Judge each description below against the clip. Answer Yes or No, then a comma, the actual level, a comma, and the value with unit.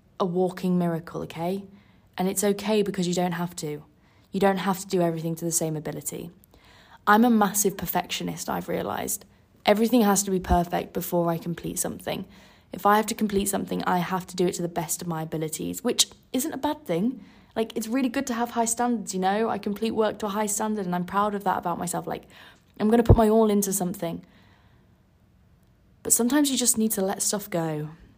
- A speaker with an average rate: No, fast, 215 wpm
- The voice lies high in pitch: Yes, high, 195 Hz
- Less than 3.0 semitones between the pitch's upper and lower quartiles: No, average, 4.0 semitones